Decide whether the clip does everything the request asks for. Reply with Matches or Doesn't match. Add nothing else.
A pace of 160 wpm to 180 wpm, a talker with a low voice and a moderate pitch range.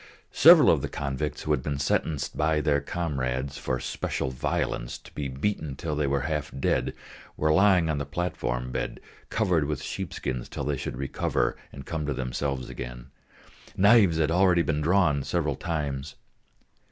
Matches